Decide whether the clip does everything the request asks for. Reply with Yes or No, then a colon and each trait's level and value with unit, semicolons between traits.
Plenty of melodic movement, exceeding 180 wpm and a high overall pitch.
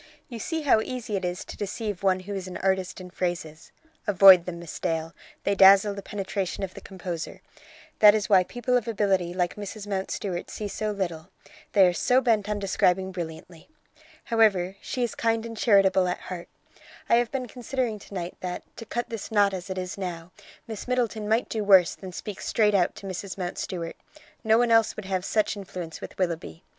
No: average, 3.2 semitones; average, 200 wpm; high, 195 Hz